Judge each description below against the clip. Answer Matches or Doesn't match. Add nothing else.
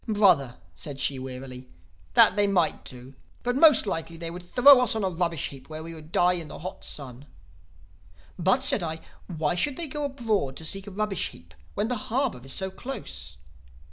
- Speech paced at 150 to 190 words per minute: Doesn't match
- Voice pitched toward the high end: Doesn't match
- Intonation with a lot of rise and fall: Matches